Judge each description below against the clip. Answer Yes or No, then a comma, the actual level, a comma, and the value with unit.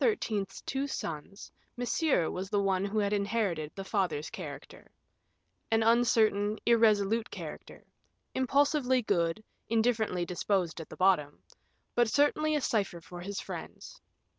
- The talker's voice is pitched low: No, high, 205 Hz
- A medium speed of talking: No, slow, 125 wpm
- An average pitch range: Yes, average, 4.2 semitones